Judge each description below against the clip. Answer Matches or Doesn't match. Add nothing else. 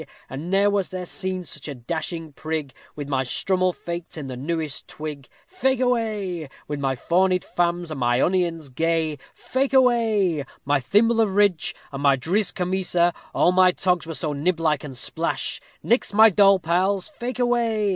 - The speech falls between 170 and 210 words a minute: Matches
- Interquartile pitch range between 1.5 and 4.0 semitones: Doesn't match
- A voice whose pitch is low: Doesn't match